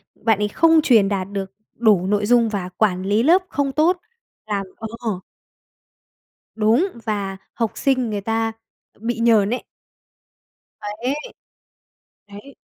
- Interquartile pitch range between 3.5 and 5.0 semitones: No, average, 3.1 semitones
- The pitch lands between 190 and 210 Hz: No, high, 220 Hz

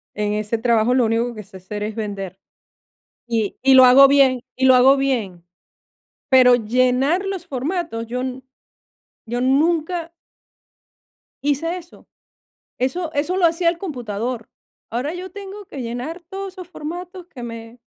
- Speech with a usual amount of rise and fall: No, wide, 6.6 semitones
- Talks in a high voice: Yes, very high, 260 Hz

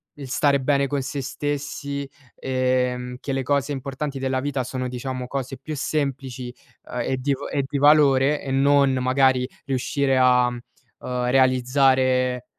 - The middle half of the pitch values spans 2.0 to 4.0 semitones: No, narrow, 1.6 semitones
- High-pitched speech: No, low, 135 Hz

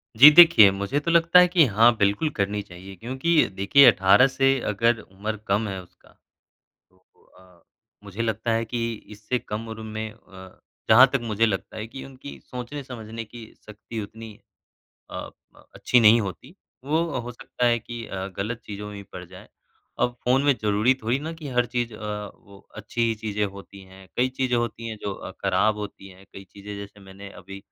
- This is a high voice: No, low, 110 Hz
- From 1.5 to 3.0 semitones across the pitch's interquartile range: No, average, 3.5 semitones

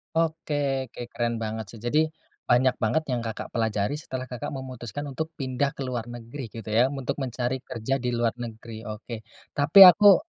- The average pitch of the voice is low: Yes, low, 125 Hz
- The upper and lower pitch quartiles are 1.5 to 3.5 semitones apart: Yes, average, 3.1 semitones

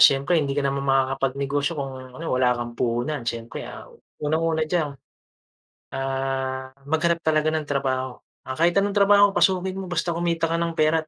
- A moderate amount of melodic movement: Yes, average, 4.0 semitones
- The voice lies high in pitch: No, medium, 145 Hz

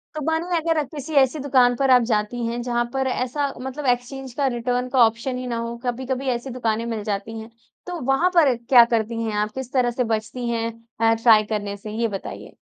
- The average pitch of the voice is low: No, high, 245 Hz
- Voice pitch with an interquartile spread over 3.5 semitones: No, narrow, 2.5 semitones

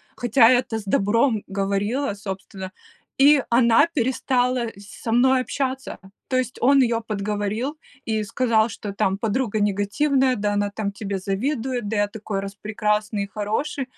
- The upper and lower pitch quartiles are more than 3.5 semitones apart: Yes, average, 4.0 semitones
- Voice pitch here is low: No, high, 220 Hz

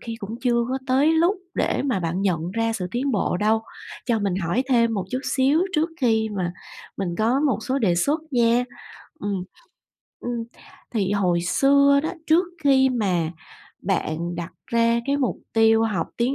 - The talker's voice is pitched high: Yes, high, 230 Hz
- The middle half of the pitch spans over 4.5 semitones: Yes, average, 5.3 semitones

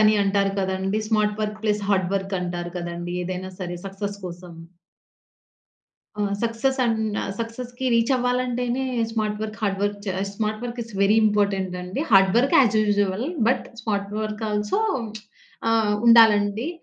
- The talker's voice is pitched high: Yes, high, 210 Hz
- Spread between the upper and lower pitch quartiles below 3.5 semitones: Yes, average, 2.8 semitones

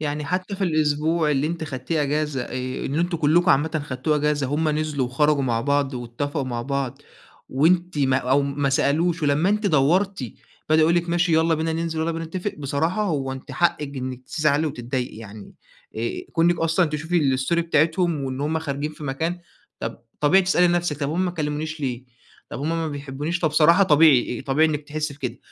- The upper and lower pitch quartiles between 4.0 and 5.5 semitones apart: No, average, 3.1 semitones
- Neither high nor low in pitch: Yes, medium, 150 Hz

